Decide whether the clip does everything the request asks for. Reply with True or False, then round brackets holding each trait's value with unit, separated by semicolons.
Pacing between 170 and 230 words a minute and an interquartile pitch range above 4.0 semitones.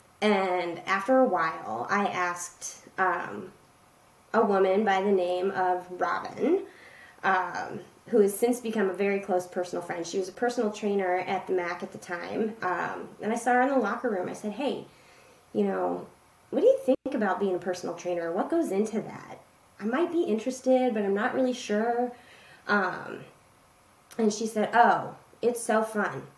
True (180 wpm; 4.6 semitones)